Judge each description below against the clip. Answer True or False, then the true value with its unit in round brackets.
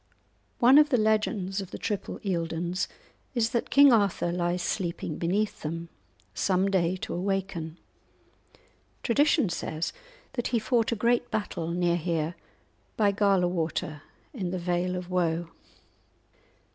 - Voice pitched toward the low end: False (185 Hz)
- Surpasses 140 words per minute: False (135 wpm)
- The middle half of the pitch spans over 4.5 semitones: False (4.0 semitones)